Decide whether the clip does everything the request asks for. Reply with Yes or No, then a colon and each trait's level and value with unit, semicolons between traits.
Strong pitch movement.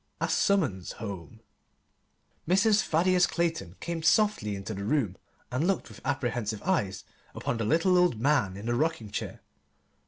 Yes: wide, 9.0 semitones